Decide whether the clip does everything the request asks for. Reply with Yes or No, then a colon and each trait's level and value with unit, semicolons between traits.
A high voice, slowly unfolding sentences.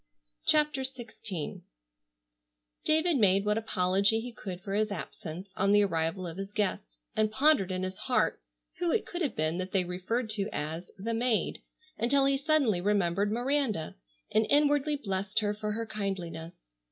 No: high, 210 Hz; average, 165 wpm